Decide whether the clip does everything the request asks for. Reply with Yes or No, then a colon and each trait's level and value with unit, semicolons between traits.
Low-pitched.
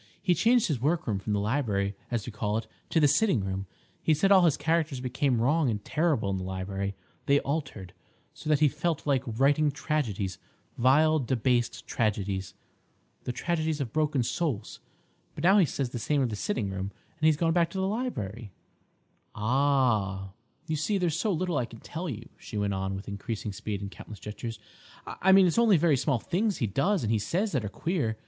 Yes: low, 130 Hz